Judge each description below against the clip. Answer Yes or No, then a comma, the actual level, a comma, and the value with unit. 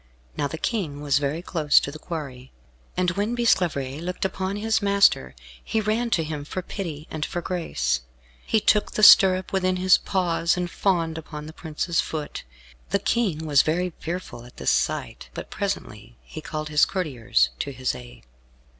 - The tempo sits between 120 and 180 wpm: Yes, average, 175 wpm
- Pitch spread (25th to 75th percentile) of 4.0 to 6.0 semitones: Yes, average, 4.5 semitones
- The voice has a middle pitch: Yes, medium, 165 Hz